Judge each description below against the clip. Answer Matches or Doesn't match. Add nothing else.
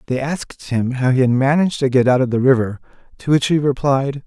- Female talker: Doesn't match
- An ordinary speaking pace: Doesn't match